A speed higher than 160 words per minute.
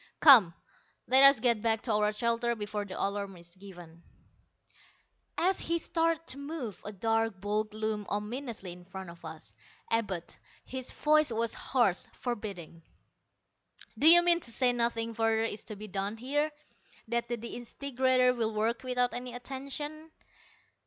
No: average, 150 wpm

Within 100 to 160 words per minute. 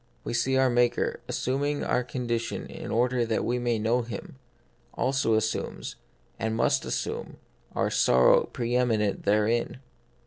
Yes: average, 145 wpm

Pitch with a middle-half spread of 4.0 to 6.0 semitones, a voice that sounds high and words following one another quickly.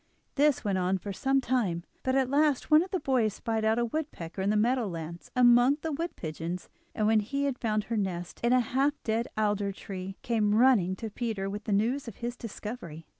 Yes: average, 4.8 semitones; high, 225 Hz; fast, 220 wpm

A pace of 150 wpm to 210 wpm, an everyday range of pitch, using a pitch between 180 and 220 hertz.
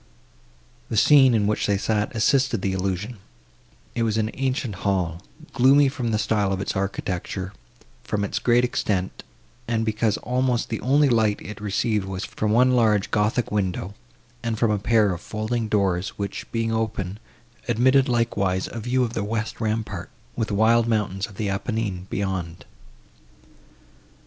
No: average, 160 wpm; average, 3.0 semitones; low, 110 Hz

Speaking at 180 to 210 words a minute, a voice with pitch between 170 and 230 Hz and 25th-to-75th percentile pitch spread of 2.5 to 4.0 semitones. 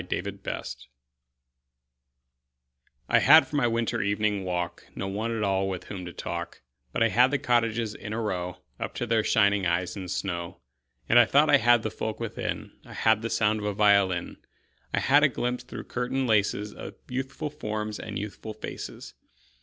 No: average, 185 wpm; low, 110 Hz; average, 3.5 semitones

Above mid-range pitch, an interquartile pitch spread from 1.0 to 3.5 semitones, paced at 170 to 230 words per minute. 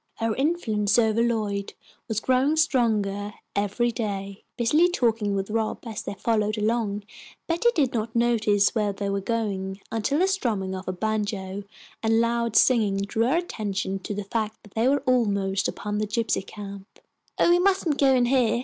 Yes: high, 220 Hz; average, 3.0 semitones; average, 175 wpm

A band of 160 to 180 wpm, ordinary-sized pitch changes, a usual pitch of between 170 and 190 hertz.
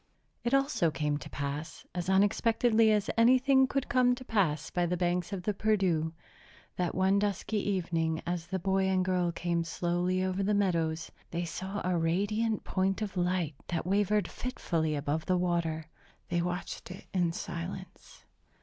Yes: average, 165 wpm; average, 3.3 semitones; medium, 185 Hz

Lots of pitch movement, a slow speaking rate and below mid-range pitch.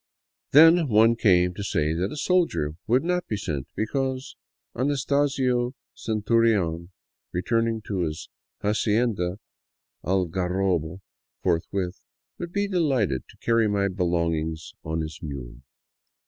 Yes: wide, 6.5 semitones; slow, 130 wpm; low, 100 Hz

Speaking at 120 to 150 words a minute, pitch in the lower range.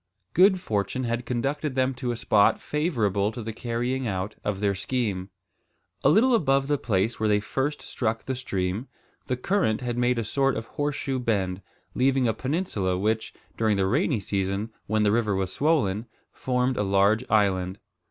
No: average, 175 wpm; low, 115 Hz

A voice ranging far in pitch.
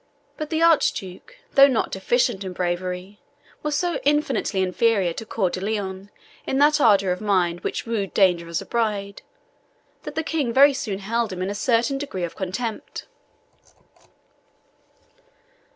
Yes: wide, 6.1 semitones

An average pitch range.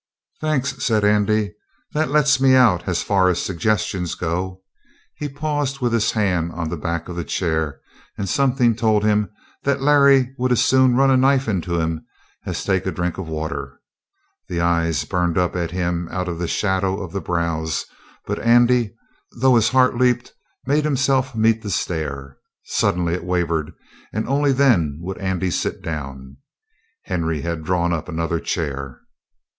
No: wide, 7.0 semitones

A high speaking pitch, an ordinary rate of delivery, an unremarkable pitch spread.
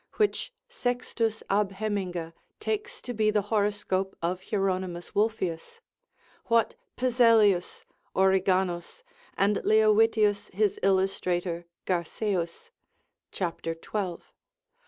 No: high, 200 Hz; slow, 90 wpm; average, 3.1 semitones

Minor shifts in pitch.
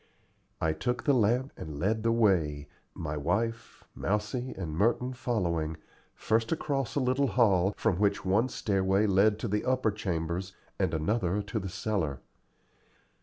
No: average, 4.8 semitones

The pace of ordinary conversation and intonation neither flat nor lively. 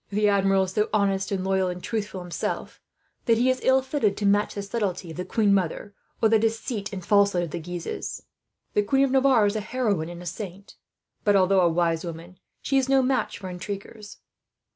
No: fast, 210 wpm; average, 3.4 semitones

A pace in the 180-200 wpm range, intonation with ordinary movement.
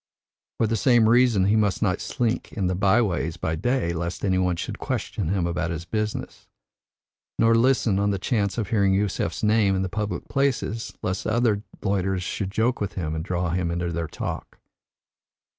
Yes: average, 185 wpm; average, 3.7 semitones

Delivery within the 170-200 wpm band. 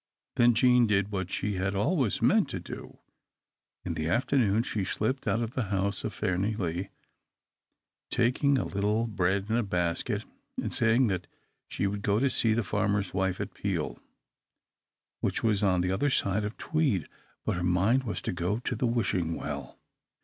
Yes: average, 175 wpm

